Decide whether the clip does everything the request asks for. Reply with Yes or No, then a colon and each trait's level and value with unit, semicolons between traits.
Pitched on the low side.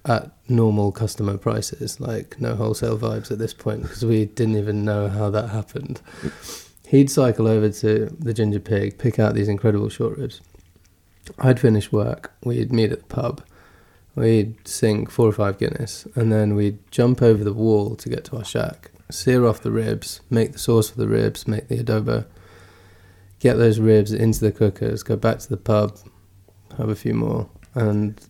Yes: low, 110 Hz